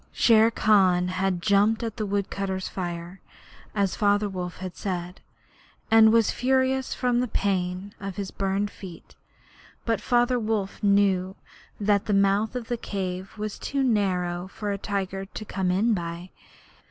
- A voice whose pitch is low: No, high, 200 Hz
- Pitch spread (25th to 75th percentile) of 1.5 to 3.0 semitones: Yes, average, 2.7 semitones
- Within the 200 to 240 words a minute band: No, average, 155 wpm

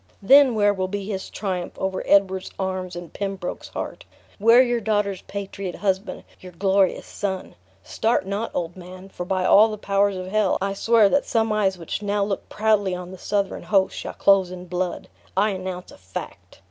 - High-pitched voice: Yes, high, 195 Hz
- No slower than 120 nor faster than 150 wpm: No, average, 185 wpm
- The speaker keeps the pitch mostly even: Yes, narrow, 1.9 semitones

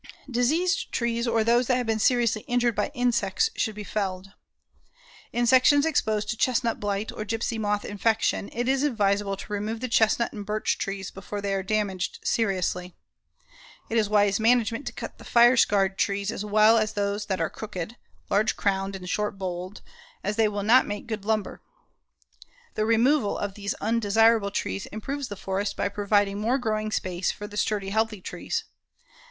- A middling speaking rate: Yes, average, 180 wpm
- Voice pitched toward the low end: No, high, 215 Hz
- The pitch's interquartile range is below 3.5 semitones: Yes, narrow, 2.5 semitones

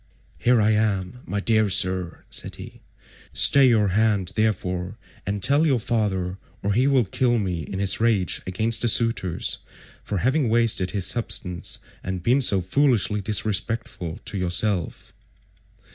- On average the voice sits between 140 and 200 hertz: No, low, 105 Hz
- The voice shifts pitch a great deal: No, average, 3.8 semitones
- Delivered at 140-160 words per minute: Yes, average, 145 wpm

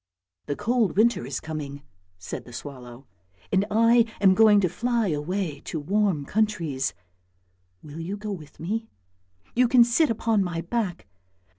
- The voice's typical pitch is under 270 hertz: Yes, high, 190 Hz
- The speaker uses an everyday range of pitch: No, wide, 7.1 semitones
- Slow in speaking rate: No, average, 160 wpm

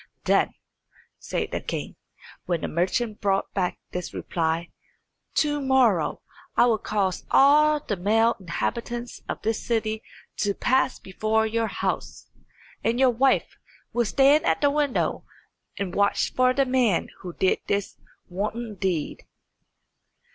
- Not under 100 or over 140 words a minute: Yes, slow, 135 wpm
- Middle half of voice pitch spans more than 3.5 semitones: Yes, average, 4.7 semitones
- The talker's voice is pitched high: Yes, high, 220 Hz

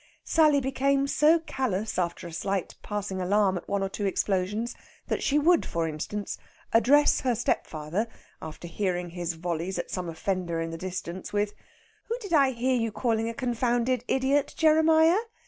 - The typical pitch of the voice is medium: No, high, 210 Hz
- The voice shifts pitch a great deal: Yes, wide, 6.7 semitones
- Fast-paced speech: No, average, 165 wpm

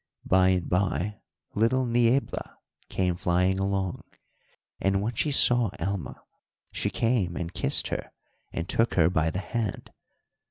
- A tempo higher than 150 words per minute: No, slow, 135 wpm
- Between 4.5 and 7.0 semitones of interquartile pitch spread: No, average, 4.1 semitones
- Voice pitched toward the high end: No, very low, 95 Hz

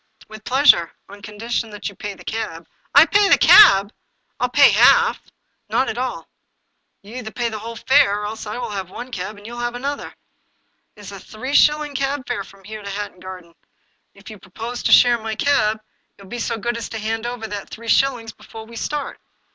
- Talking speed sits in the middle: No, fast, 235 wpm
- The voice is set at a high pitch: Yes, high, 225 Hz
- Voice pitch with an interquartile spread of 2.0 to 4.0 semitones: Yes, average, 3.1 semitones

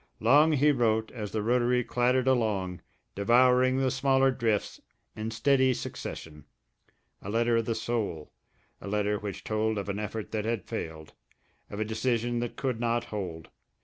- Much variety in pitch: No, average, 3.2 semitones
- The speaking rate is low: No, average, 160 wpm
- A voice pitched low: Yes, low, 115 Hz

